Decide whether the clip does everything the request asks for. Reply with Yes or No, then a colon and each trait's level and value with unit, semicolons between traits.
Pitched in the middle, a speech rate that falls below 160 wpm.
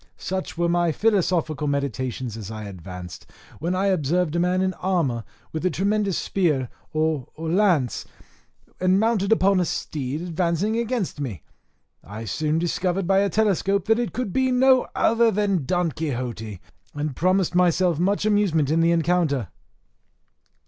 Yes: medium, 175 Hz; average, 150 wpm